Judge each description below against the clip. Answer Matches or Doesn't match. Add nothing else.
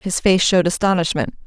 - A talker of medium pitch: Matches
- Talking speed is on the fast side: Doesn't match